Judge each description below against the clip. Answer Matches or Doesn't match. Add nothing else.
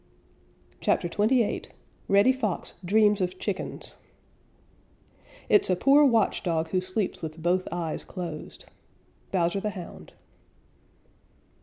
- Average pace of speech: Doesn't match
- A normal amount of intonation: Matches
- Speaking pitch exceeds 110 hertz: Matches